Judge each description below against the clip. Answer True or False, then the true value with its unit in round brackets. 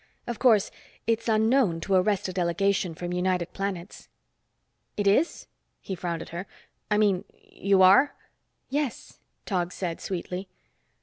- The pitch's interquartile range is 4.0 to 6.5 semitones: False (3.5 semitones)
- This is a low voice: False (195 Hz)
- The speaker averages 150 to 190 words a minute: False (135 wpm)